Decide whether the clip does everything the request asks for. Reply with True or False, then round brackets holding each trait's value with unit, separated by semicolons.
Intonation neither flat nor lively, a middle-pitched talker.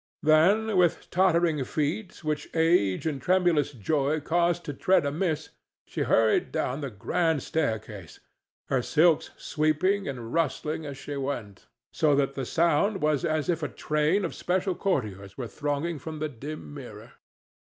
True (3.8 semitones; 155 Hz)